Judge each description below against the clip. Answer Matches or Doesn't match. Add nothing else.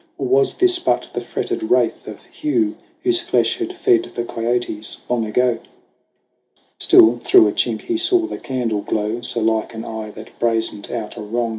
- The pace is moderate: Matches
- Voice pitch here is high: Doesn't match